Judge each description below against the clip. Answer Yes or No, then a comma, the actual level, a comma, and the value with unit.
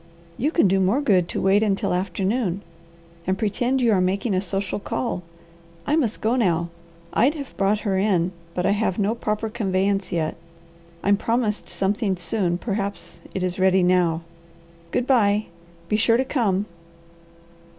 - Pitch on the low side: No, high, 200 Hz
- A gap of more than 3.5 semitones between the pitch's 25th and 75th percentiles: No, average, 3.2 semitones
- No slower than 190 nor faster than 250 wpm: No, average, 160 wpm